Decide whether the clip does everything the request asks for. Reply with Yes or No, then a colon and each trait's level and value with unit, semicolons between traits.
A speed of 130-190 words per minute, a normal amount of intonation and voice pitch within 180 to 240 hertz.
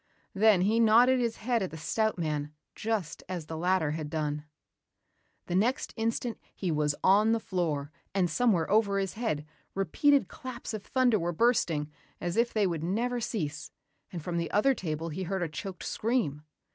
No: average, 180 wpm; wide, 5.8 semitones; high, 190 Hz